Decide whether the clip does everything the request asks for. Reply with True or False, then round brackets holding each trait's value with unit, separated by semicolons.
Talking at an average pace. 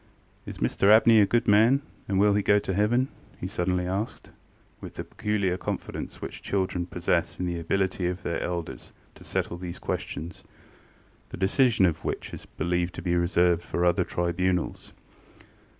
True (165 wpm)